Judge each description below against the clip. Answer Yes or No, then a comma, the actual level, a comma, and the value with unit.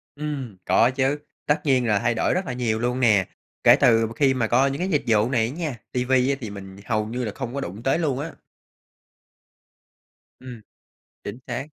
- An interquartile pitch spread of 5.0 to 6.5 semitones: No, average, 3.4 semitones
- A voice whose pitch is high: No, low, 125 Hz